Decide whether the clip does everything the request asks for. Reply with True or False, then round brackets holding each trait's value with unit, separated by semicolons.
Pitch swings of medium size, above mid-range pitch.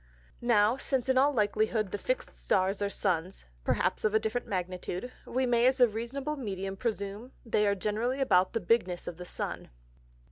True (4.2 semitones; 215 Hz)